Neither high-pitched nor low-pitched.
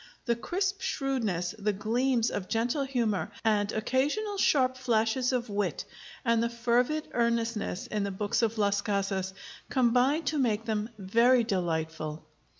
No: high, 230 Hz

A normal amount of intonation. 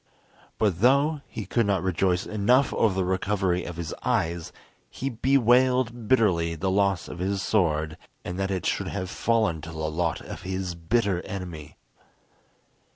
Yes: average, 4.5 semitones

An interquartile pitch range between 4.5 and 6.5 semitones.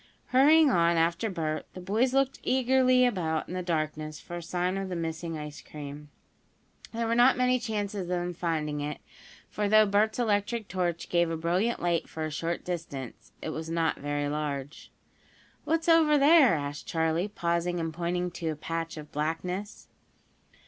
Yes: average, 5.2 semitones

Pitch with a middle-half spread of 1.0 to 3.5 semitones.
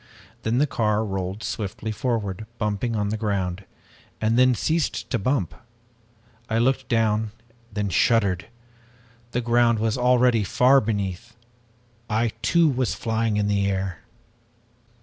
Yes: average, 3.0 semitones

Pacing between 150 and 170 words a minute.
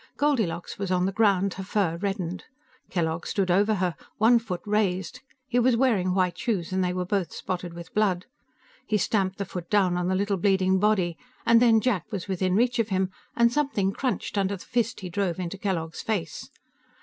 No: average, 195 wpm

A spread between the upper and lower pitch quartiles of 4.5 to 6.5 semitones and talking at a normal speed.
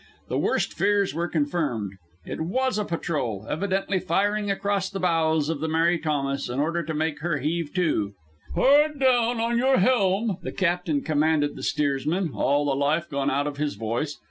Yes: average, 5.2 semitones; average, 185 wpm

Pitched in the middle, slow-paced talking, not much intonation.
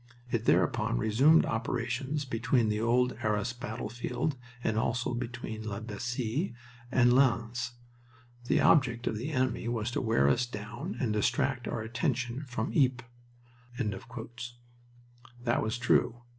No: low, 120 Hz; slow, 130 wpm; narrow, 1.9 semitones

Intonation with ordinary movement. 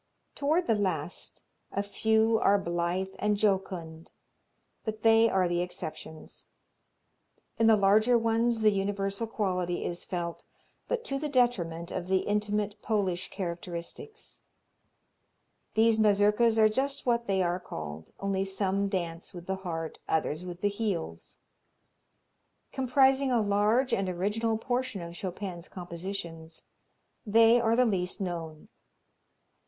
Yes: average, 4.2 semitones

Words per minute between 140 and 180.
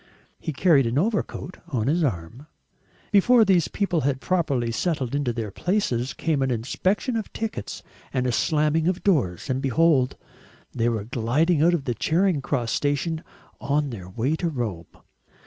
Yes: average, 160 wpm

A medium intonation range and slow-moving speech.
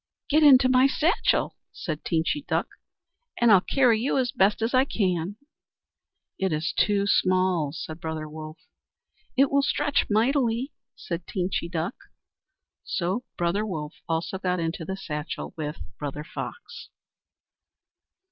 No: wide, 7.3 semitones; slow, 130 wpm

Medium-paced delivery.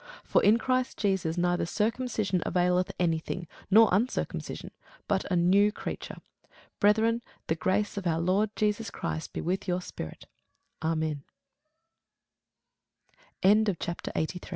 No: slow, 125 wpm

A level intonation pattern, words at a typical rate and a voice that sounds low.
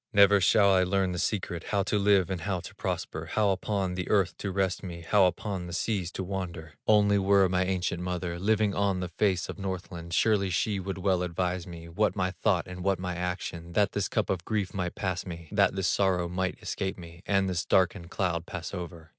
No: narrow, 2.1 semitones; fast, 220 wpm; very low, 95 Hz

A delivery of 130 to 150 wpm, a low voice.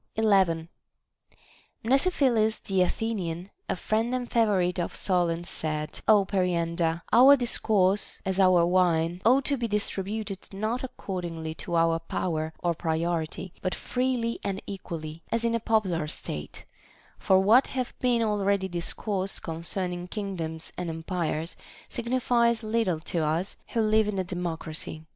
No: average, 140 wpm; high, 190 Hz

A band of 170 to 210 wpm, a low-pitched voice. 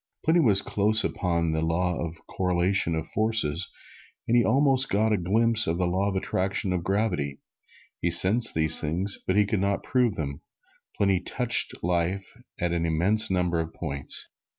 Yes: average, 175 wpm; very low, 95 Hz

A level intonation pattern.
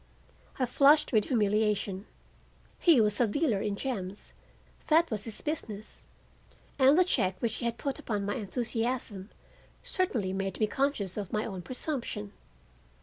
No: average, 4.7 semitones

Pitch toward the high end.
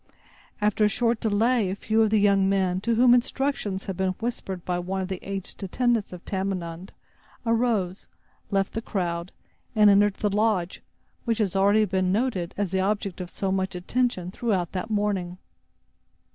Yes: high, 195 Hz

